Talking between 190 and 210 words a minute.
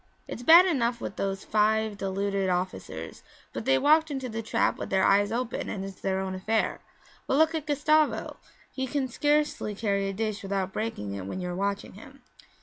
Yes: average, 195 wpm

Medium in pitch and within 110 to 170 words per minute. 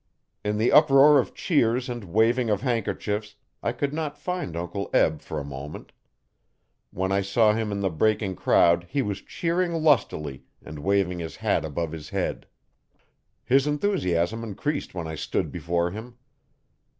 No: low, 105 Hz; average, 160 wpm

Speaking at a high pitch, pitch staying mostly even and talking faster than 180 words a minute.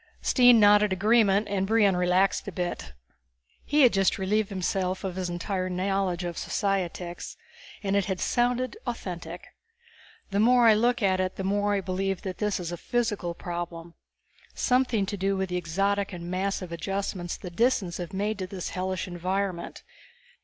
No: high, 195 Hz; narrow, 2.3 semitones; average, 165 wpm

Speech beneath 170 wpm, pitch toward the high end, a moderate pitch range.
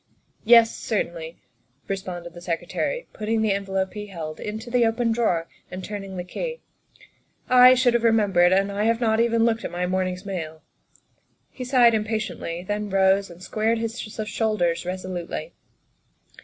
Yes: average, 160 wpm; high, 205 Hz; average, 3.9 semitones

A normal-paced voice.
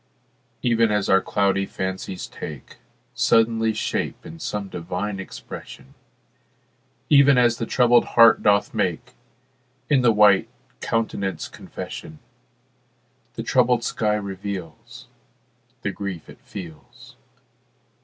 No: slow, 105 wpm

